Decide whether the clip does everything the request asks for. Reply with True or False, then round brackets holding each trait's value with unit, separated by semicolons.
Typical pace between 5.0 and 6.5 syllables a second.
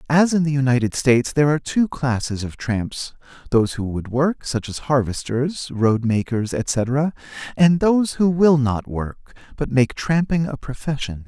False (4.6 syllables/s)